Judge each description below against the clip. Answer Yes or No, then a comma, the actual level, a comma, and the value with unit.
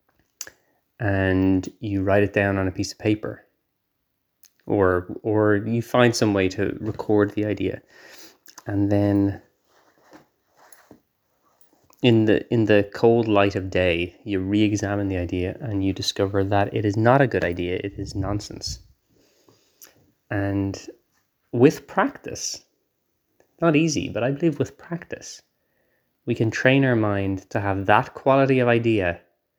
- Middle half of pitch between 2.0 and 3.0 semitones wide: Yes, average, 2.7 semitones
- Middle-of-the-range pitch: No, low, 100 Hz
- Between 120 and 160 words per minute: Yes, average, 140 wpm